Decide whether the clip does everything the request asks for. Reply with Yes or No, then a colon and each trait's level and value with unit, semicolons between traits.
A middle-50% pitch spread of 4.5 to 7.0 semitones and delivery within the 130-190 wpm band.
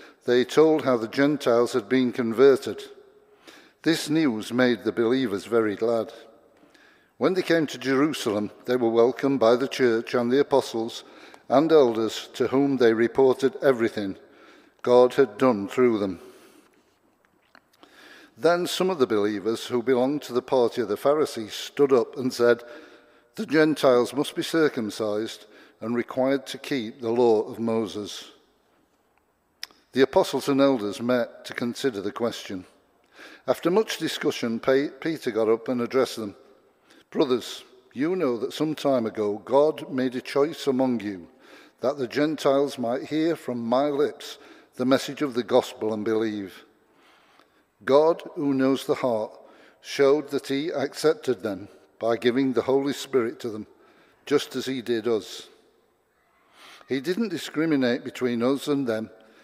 No: average, 3.9 semitones; average, 145 wpm